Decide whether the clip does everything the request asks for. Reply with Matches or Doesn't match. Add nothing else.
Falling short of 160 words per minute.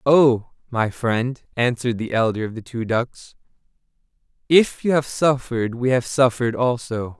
Matches